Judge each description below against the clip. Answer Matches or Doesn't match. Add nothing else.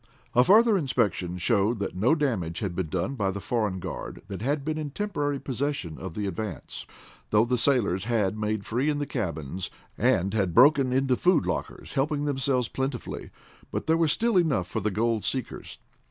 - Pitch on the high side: Doesn't match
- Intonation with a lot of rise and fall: Matches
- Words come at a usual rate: Matches